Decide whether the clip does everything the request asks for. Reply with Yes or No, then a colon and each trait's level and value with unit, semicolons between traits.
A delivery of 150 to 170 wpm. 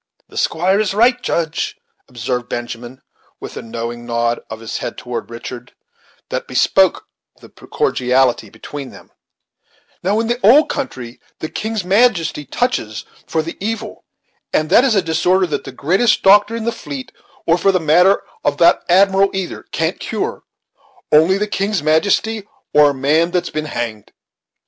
Yes: average, 160 wpm